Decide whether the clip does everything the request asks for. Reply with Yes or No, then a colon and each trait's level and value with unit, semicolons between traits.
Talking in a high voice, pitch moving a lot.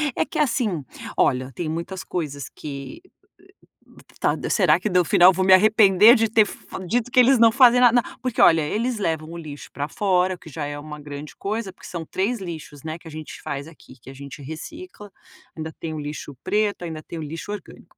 No: medium, 175 Hz; wide, 5.9 semitones